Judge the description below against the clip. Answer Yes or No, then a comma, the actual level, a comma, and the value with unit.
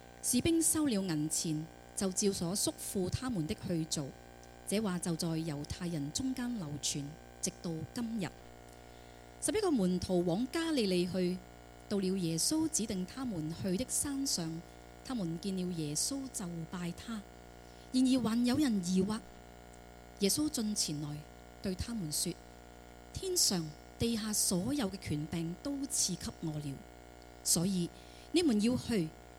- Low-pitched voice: No, medium, 170 Hz